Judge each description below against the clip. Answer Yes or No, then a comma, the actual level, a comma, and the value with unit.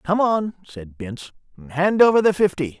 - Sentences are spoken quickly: No, average, 170 wpm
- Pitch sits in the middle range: Yes, medium, 170 Hz